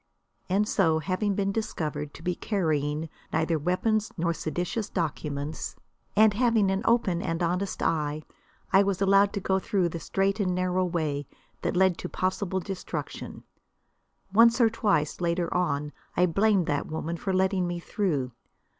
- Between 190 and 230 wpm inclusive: No, average, 155 wpm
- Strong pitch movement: No, average, 3.5 semitones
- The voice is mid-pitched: Yes, medium, 180 Hz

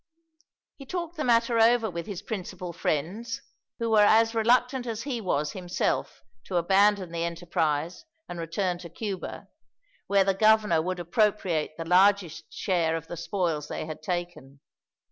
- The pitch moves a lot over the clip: No, average, 4.6 semitones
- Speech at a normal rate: Yes, average, 155 wpm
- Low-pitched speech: No, medium, 185 Hz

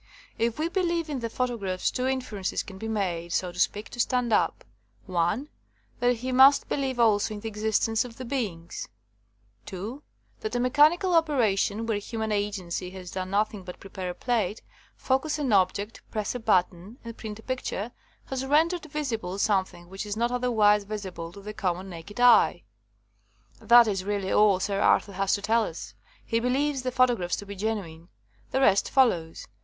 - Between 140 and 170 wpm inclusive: No, average, 180 wpm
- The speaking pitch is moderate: No, high, 215 Hz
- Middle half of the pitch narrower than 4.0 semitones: No, average, 4.5 semitones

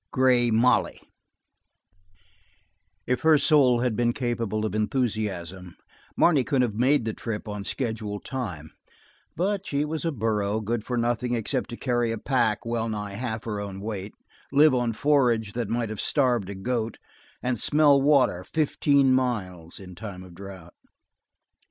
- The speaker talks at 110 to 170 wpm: Yes, average, 155 wpm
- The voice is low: Yes, low, 115 Hz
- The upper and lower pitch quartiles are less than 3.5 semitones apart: No, average, 3.8 semitones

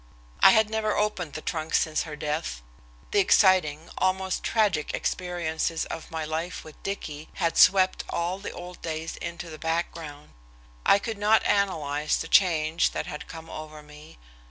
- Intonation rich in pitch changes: No, average, 3.4 semitones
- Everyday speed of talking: Yes, average, 160 wpm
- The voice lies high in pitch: No, medium, 165 Hz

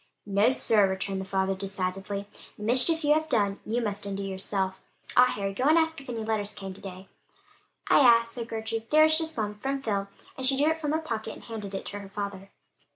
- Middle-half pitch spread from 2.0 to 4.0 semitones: No, average, 4.7 semitones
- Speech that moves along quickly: Yes, fast, 225 wpm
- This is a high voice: Yes, high, 215 Hz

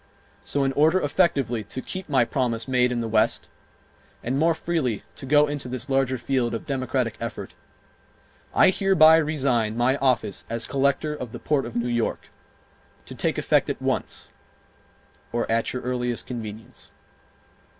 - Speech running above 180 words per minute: No, average, 160 wpm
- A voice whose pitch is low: Yes, low, 130 Hz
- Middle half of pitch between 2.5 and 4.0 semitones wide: Yes, average, 3.6 semitones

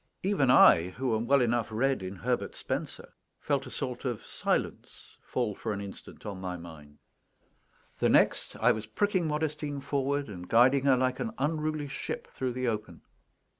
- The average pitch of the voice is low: Yes, low, 125 Hz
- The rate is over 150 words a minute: Yes, average, 170 wpm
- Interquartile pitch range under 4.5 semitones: No, average, 5.0 semitones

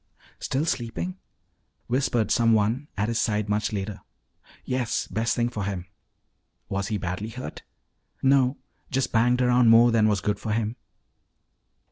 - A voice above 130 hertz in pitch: No, low, 115 Hz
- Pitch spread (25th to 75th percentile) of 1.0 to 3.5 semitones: Yes, average, 2.9 semitones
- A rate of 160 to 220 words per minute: No, average, 145 wpm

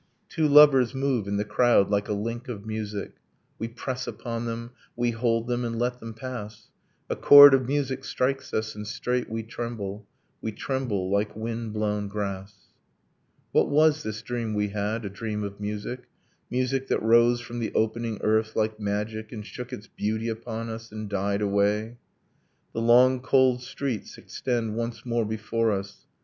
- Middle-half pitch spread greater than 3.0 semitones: No, narrow, 2.5 semitones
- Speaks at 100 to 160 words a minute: No, average, 170 wpm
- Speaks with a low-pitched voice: Yes, low, 115 Hz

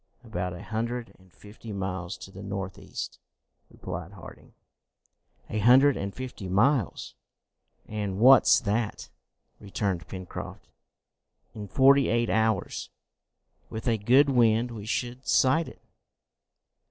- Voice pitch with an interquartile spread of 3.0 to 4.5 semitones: Yes, average, 4.0 semitones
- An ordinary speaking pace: No, slow, 120 wpm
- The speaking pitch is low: Yes, low, 110 Hz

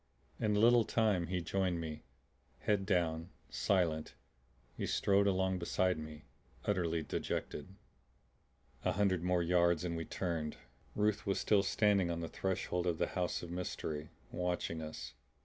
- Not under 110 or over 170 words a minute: Yes, average, 150 wpm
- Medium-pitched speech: No, very low, 90 Hz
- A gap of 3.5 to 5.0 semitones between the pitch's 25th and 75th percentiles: No, average, 2.7 semitones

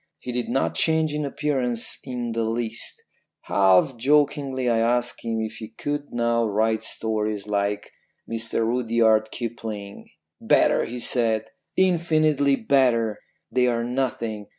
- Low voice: Yes, low, 115 Hz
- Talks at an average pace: No, slow, 130 wpm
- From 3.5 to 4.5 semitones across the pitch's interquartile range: No, average, 3.1 semitones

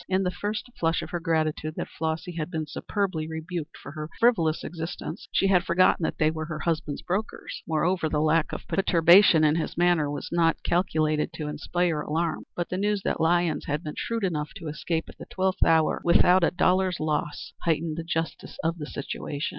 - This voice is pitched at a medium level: Yes, medium, 165 Hz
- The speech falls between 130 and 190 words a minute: No, average, 200 wpm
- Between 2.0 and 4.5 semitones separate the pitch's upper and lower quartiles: Yes, narrow, 2.4 semitones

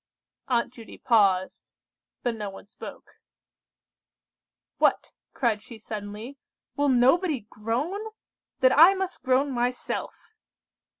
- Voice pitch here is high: Yes, high, 245 Hz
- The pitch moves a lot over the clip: No, average, 4.5 semitones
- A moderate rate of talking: No, slow, 105 wpm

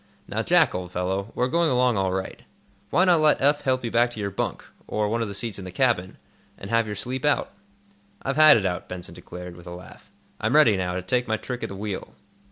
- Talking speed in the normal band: No, fast, 245 wpm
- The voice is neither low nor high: No, low, 110 Hz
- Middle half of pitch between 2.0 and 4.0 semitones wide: No, average, 5.2 semitones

